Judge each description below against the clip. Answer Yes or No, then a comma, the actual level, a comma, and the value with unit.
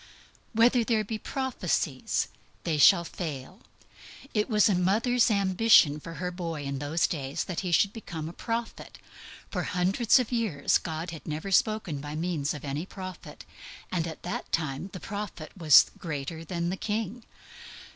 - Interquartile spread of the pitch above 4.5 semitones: Yes, average, 5.1 semitones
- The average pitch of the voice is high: No, medium, 180 Hz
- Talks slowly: No, average, 165 wpm